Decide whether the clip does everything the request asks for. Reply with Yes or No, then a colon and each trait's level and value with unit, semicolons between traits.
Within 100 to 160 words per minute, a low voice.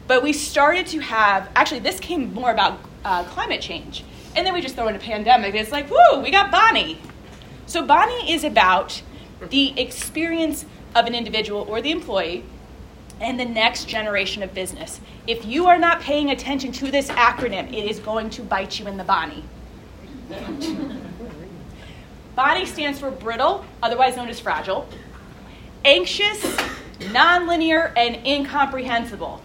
No: average, 155 wpm; very high, 260 Hz